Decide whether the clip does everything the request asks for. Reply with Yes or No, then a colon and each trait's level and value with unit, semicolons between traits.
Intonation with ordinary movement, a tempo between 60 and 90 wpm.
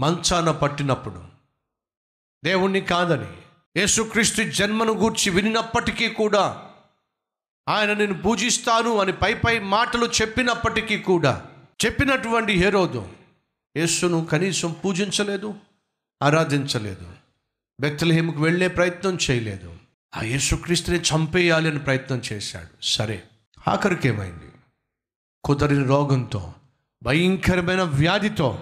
No: wide, 6.9 semitones; average, 85 wpm